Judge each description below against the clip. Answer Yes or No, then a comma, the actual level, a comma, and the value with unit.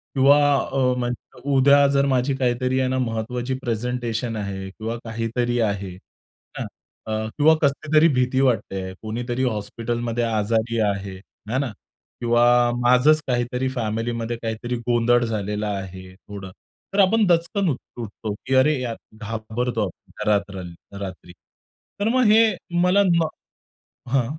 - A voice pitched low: Yes, low, 120 Hz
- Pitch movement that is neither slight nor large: Yes, average, 3.2 semitones